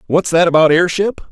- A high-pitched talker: No, medium, 170 Hz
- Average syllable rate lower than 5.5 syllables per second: No, 5.6 syllables/s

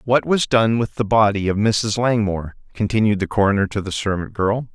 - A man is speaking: Yes, male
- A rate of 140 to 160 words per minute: No, average, 200 wpm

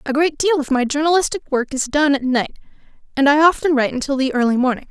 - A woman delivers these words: Yes, female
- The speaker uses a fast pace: Yes, fast, 235 wpm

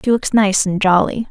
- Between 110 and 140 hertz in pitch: No, high, 205 Hz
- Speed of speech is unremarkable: No, fast, 230 wpm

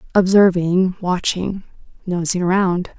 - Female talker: Yes, female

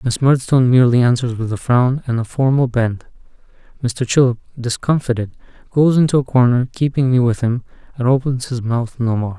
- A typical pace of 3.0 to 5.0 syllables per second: No, 5.6 syllables/s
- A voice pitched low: Yes, low, 125 Hz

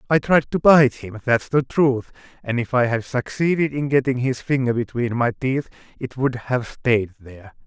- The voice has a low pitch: Yes, low, 130 Hz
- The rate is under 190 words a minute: No, average, 195 wpm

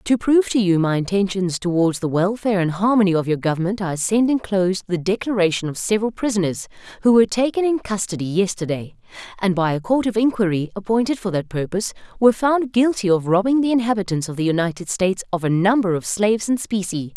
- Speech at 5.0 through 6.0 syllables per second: No, 6.3 syllables/s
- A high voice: Yes, high, 200 Hz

